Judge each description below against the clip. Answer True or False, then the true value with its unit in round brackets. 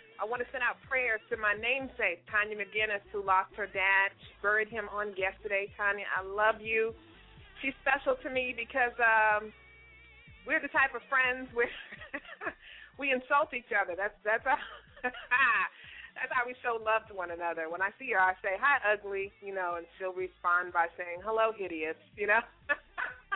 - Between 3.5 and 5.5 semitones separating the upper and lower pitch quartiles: True (4.4 semitones)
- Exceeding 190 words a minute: False (180 wpm)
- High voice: True (215 Hz)